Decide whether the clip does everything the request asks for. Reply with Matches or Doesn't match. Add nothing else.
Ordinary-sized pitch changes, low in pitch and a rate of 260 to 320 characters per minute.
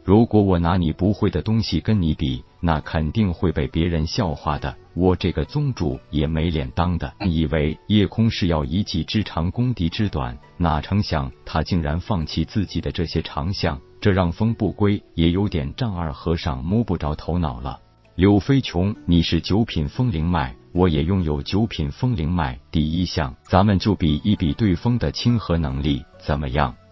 Matches